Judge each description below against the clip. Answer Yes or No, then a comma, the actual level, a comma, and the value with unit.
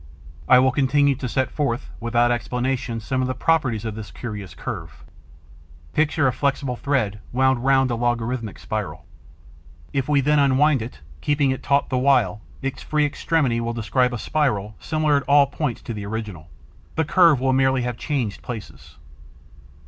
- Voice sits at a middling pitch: No, low, 130 Hz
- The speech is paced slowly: No, average, 170 wpm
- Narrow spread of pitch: No, average, 3.2 semitones